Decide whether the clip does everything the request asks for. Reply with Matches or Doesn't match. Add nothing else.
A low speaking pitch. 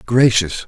Matches